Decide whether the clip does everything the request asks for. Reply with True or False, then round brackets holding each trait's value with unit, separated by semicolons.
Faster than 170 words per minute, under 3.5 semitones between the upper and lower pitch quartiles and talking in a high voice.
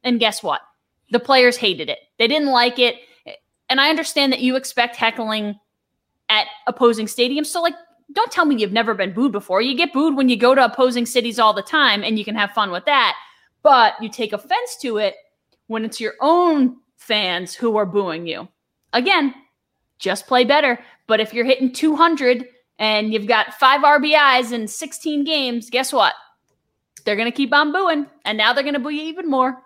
False (195 wpm; 4.8 semitones; 250 Hz)